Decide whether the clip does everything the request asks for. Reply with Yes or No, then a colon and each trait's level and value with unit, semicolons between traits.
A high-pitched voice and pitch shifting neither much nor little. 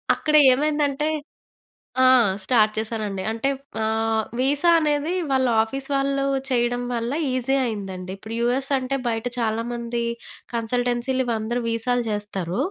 Yes: high, 240 Hz; average, 3.3 semitones